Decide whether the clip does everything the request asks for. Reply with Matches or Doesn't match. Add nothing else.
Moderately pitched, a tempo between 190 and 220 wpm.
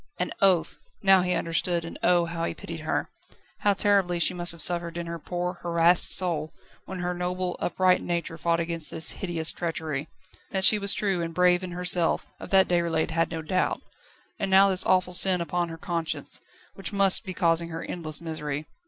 Matches